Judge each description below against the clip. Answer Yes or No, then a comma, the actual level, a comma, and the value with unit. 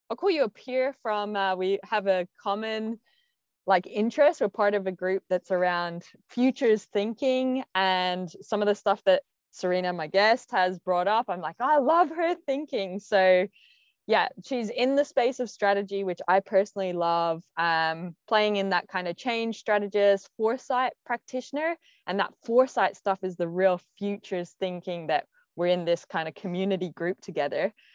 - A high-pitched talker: Yes, high, 200 Hz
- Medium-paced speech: Yes, average, 175 wpm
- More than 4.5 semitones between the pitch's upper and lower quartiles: Yes, average, 5.2 semitones